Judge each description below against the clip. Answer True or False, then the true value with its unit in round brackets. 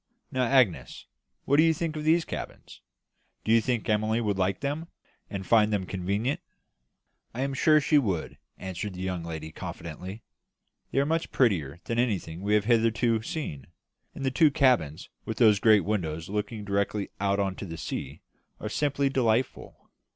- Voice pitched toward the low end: True (110 Hz)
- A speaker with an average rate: True (175 wpm)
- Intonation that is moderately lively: False (5.7 semitones)